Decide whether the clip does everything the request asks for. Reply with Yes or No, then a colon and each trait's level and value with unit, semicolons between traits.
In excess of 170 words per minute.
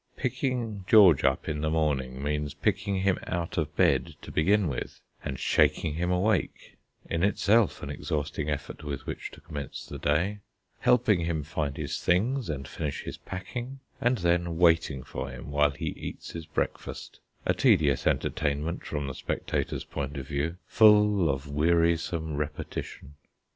No: average, 160 wpm